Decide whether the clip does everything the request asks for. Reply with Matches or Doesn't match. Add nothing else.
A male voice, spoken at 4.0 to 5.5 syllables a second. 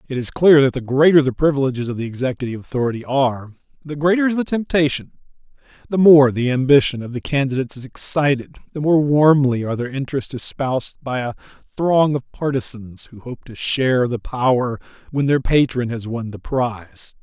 Doesn't match